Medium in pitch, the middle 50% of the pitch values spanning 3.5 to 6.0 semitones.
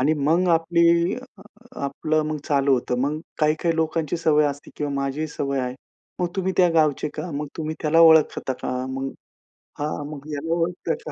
No: medium, 155 Hz; narrow, 2.6 semitones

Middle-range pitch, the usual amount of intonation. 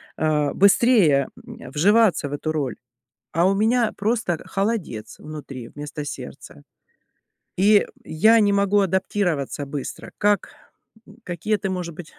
No: medium, 180 Hz; wide, 5.7 semitones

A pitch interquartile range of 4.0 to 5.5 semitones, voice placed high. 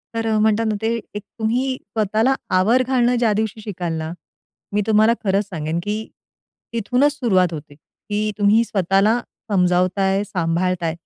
No: average, 3.5 semitones; high, 210 Hz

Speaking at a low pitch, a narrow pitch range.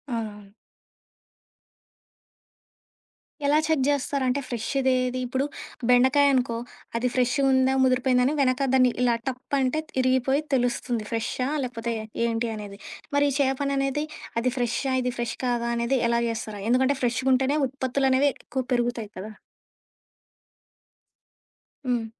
No: very high, 255 Hz; narrow, 2.1 semitones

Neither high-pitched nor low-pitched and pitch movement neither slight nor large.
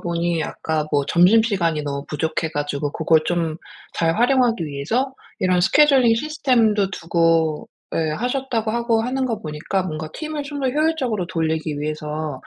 No: medium, 175 Hz; wide, 7.5 semitones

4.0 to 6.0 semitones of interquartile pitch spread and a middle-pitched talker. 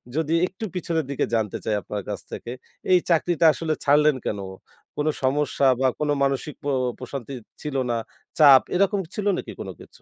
No: average, 3.6 semitones; medium, 150 Hz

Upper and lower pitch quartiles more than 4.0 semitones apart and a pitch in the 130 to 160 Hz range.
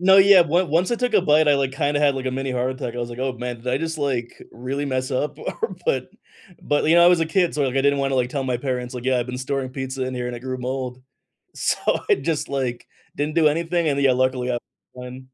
No: average, 3.1 semitones; low, 135 Hz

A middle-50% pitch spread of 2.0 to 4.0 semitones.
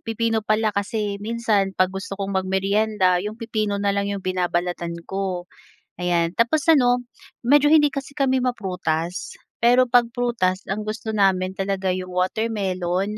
Yes: average, 3.6 semitones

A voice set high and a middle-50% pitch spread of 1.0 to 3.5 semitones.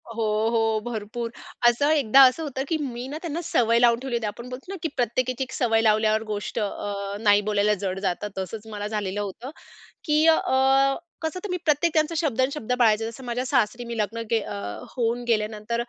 No: high, 235 Hz; average, 3.9 semitones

